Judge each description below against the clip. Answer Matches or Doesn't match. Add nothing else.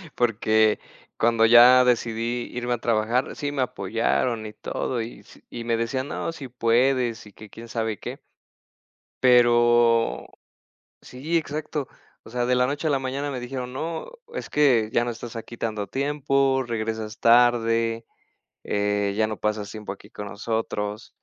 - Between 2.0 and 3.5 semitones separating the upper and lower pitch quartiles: Matches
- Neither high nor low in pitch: Doesn't match